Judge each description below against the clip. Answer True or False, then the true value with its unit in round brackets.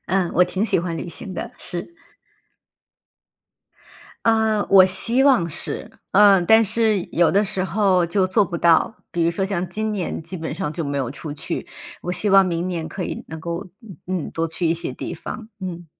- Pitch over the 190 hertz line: False (185 Hz)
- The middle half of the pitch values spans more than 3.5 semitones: False (3.1 semitones)